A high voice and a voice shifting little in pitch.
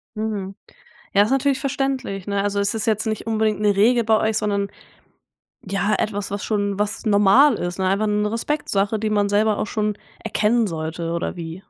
Yes: high, 210 Hz; narrow, 1.8 semitones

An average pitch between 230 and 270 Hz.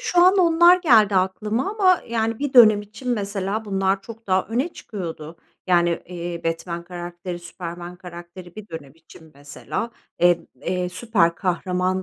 No: medium, 185 Hz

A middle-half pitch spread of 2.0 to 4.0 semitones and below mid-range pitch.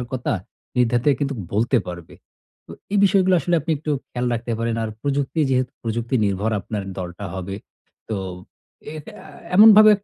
No: average, 4.6 semitones; low, 120 Hz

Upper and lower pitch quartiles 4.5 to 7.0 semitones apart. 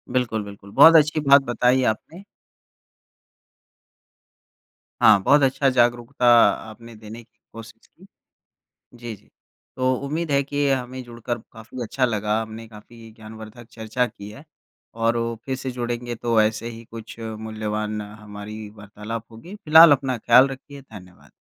No: average, 3.0 semitones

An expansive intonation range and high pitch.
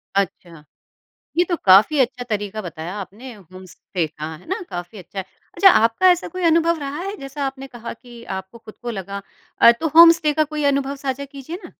Yes: wide, 7.7 semitones; high, 245 Hz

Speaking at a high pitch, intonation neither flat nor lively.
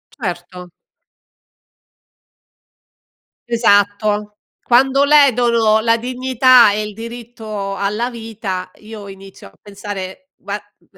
Yes: high, 215 Hz; average, 3.0 semitones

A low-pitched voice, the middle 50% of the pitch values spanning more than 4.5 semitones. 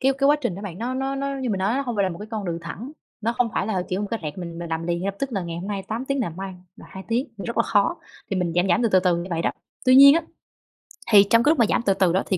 No: high, 200 Hz; average, 5.2 semitones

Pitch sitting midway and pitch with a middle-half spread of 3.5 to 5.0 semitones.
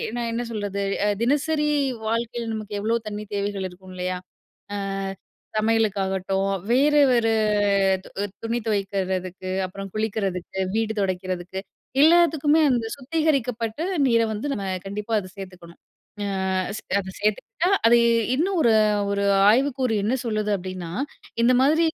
No: high, 215 Hz; average, 4.0 semitones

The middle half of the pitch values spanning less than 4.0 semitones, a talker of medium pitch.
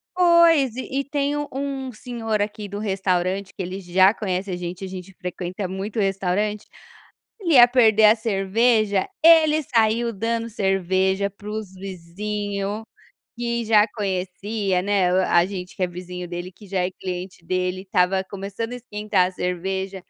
No: average, 3.4 semitones; high, 200 Hz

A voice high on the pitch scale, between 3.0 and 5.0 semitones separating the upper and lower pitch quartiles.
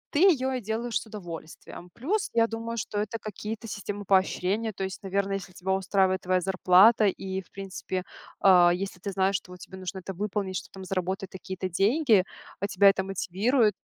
No: high, 195 Hz; narrow, 2.4 semitones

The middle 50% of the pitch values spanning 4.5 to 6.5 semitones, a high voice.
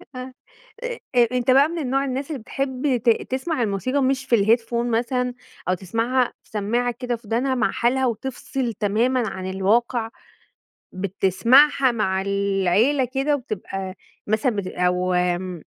Yes: average, 4.8 semitones; high, 235 Hz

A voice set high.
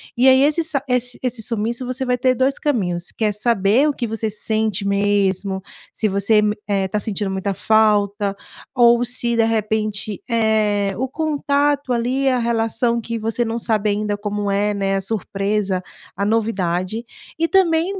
Yes: high, 220 Hz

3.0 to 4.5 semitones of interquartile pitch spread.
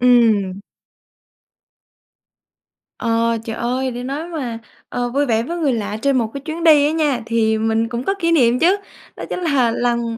Yes: average, 4.0 semitones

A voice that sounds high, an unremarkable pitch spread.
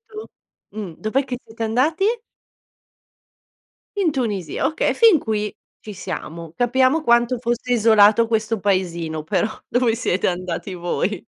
Yes: high, 220 Hz; average, 4.7 semitones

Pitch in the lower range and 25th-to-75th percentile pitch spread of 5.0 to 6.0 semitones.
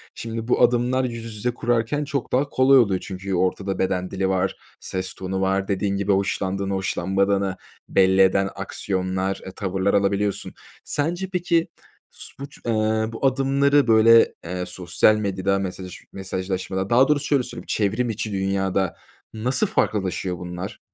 No: low, 100 Hz; average, 4.1 semitones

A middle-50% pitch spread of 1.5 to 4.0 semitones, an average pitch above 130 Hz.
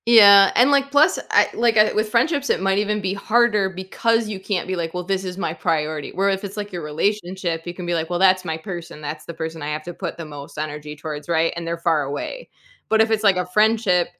No: average, 4.5 semitones; medium, 185 Hz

